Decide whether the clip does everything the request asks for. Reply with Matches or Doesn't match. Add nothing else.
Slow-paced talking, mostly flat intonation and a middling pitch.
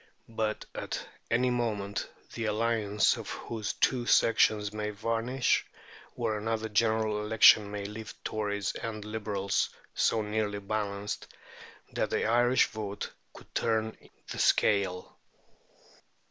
Doesn't match